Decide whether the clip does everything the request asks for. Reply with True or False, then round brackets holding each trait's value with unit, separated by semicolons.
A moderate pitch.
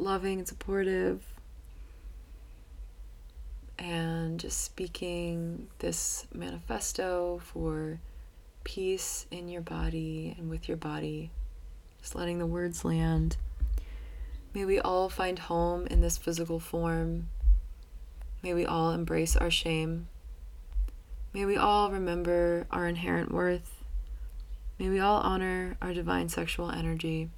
True (160 Hz)